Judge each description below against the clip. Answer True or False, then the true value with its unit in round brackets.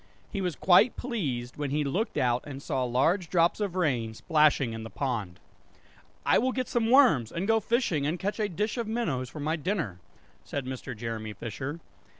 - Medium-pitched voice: True (150 Hz)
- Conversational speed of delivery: True (190 wpm)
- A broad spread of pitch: True (8.3 semitones)